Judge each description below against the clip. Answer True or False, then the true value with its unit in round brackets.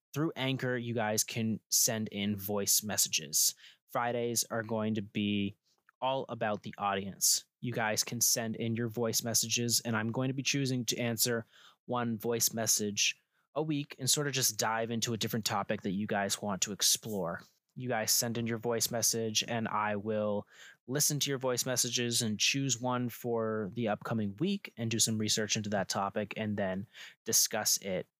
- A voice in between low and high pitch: False (115 Hz)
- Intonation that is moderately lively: False (2.3 semitones)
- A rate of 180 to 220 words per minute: True (185 wpm)